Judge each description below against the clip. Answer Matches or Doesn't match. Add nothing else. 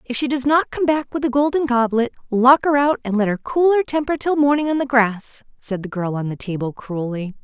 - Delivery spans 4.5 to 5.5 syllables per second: Matches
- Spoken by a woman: Matches